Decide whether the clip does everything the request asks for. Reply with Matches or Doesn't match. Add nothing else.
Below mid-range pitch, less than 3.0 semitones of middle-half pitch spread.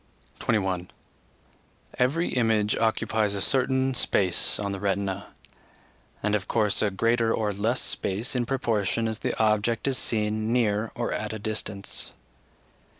Matches